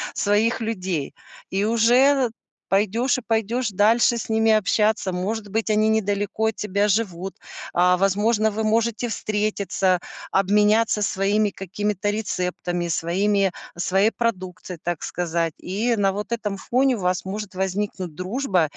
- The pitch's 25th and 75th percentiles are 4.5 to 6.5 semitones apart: No, average, 2.8 semitones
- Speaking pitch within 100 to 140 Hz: No, high, 205 Hz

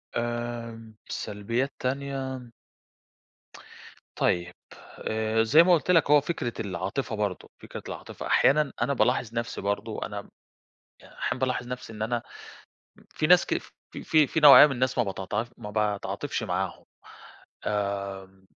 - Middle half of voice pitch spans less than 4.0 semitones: No, average, 4.4 semitones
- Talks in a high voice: No, low, 120 Hz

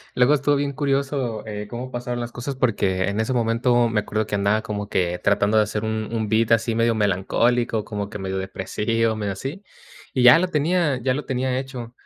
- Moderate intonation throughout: Yes, average, 3.4 semitones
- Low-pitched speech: Yes, low, 115 Hz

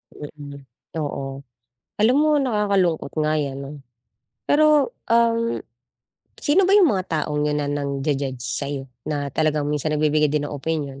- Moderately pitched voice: Yes, medium, 150 Hz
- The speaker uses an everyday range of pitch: No, wide, 6.8 semitones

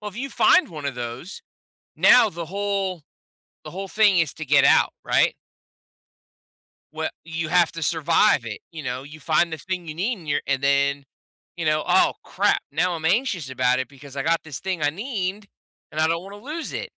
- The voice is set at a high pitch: No, medium, 165 Hz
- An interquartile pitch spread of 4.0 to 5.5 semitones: Yes, average, 5.0 semitones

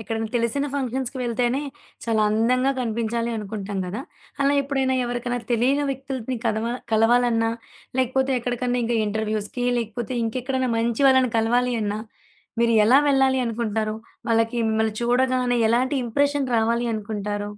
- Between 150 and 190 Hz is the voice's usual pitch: No, high, 235 Hz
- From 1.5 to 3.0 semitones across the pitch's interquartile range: Yes, narrow, 2.6 semitones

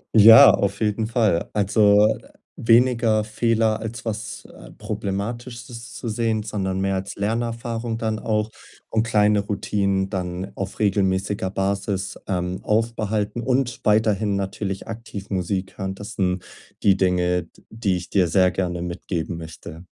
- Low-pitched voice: Yes, low, 105 Hz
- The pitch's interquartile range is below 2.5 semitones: No, average, 2.8 semitones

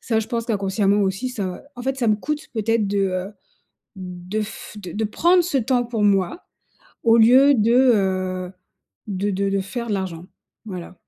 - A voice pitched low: No, high, 210 Hz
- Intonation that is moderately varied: Yes, average, 3.7 semitones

